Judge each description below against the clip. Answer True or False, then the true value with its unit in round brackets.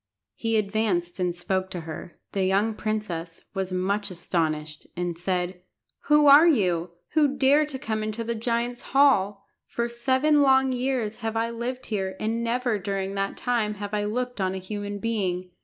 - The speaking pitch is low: False (210 Hz)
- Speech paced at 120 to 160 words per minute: False (175 wpm)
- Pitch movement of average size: True (4.4 semitones)